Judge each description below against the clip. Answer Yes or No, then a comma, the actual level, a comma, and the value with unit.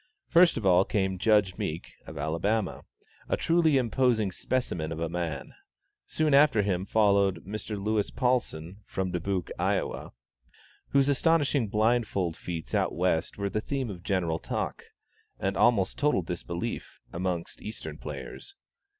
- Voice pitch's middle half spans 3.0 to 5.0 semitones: No, wide, 5.5 semitones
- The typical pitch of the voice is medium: No, low, 100 Hz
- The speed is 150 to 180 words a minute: No, average, 140 wpm